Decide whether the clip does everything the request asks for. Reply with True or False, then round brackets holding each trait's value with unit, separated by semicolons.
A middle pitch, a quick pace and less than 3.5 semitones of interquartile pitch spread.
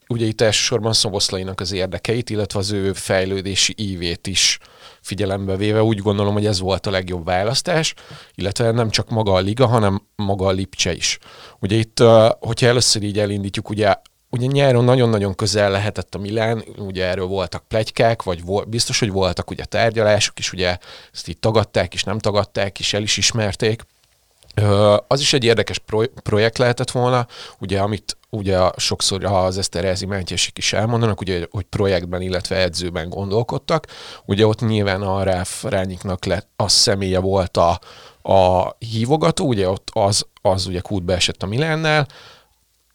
False (100 Hz; 165 wpm; 3.0 semitones)